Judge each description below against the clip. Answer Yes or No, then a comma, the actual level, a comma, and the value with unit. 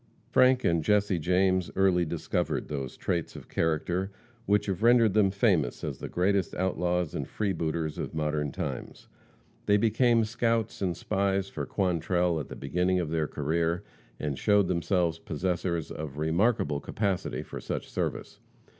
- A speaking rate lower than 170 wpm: Yes, average, 150 wpm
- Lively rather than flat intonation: No, average, 3.7 semitones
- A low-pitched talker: Yes, very low, 90 Hz